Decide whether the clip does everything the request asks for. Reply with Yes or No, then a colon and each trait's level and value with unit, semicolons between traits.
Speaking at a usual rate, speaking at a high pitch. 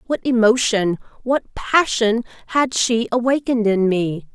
No: slow, 125 wpm; high, 230 Hz